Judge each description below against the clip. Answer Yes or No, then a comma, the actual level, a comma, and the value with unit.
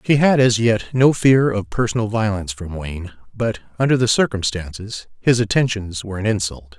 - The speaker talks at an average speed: Yes, average, 175 wpm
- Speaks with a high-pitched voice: No, low, 110 Hz